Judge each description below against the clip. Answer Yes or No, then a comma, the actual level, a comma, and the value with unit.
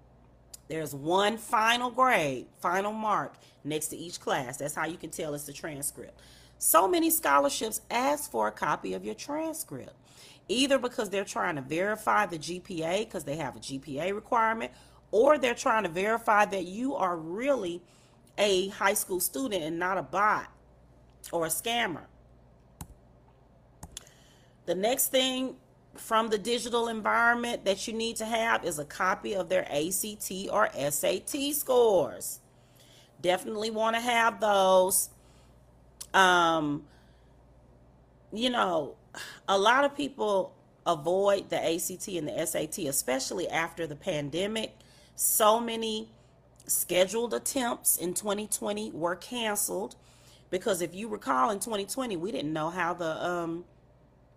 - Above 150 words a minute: No, average, 140 wpm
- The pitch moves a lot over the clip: Yes, wide, 5.7 semitones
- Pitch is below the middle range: No, high, 190 Hz